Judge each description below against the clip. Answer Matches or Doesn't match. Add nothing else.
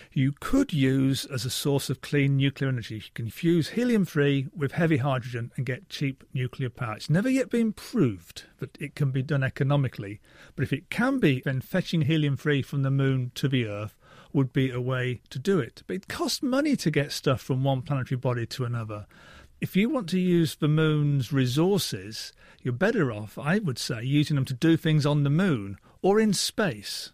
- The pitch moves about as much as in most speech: Matches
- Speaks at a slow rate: Doesn't match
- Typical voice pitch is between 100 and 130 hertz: Doesn't match